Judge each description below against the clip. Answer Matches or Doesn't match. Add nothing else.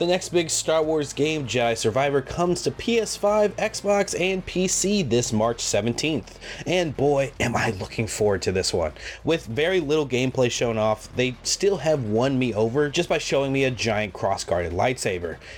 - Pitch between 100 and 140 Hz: Matches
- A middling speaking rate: Matches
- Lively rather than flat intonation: Matches